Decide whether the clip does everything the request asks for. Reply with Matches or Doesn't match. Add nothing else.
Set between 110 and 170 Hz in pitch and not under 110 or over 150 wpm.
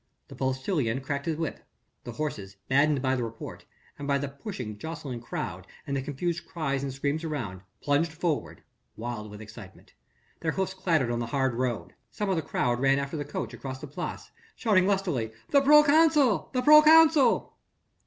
Doesn't match